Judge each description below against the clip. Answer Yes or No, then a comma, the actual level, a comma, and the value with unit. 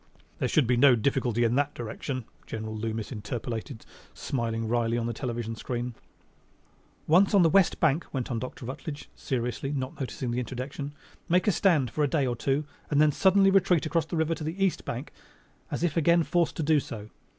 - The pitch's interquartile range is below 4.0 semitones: No, average, 5.1 semitones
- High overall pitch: No, low, 135 Hz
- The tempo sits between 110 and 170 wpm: No, average, 195 wpm